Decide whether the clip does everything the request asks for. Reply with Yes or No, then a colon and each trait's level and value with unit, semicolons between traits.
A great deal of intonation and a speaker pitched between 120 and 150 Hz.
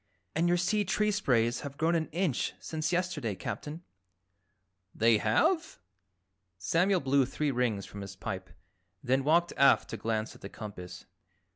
Yes: wide, 7.8 semitones; medium, 140 Hz